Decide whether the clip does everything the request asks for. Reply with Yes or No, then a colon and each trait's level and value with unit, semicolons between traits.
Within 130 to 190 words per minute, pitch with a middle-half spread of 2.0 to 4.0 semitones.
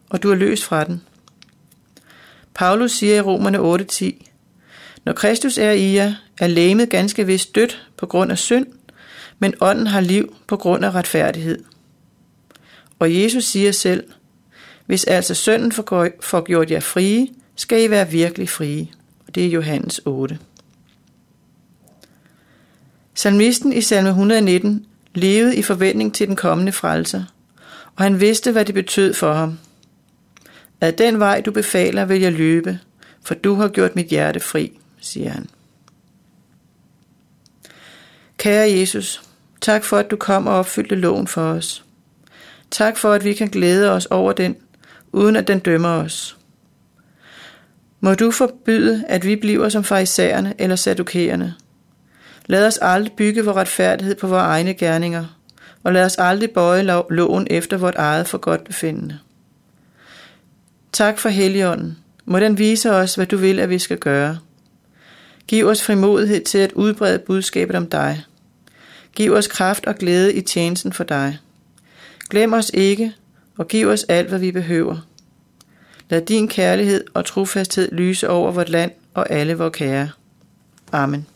Yes: average, 150 wpm; average, 3.7 semitones